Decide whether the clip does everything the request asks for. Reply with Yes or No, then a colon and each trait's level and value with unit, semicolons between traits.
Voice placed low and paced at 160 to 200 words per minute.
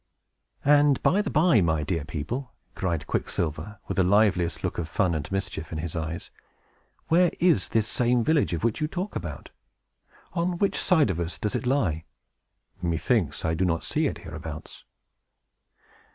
Yes: very low, 95 Hz; average, 165 wpm